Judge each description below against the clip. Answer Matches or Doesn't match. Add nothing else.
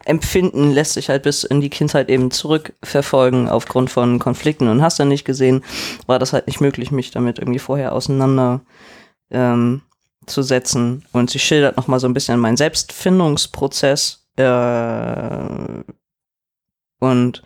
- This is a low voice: Matches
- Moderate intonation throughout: Doesn't match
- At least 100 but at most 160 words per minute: Matches